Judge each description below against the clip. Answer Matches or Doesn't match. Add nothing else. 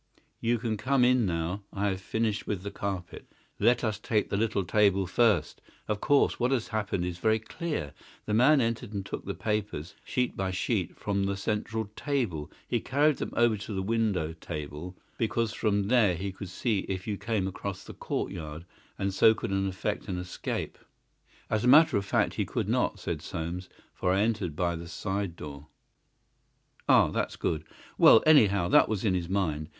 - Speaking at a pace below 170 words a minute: Doesn't match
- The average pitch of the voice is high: Doesn't match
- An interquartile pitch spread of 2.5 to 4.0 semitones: Matches